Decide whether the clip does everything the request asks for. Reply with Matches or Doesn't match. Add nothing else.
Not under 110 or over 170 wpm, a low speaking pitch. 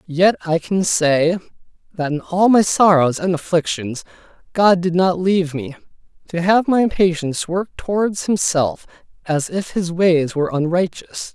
Doesn't match